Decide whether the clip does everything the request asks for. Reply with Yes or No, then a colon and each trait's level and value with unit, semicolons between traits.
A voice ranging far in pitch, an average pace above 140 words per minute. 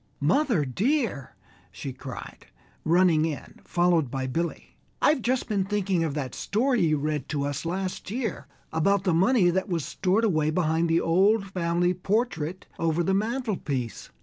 No: average, 4.6 semitones; average, 155 wpm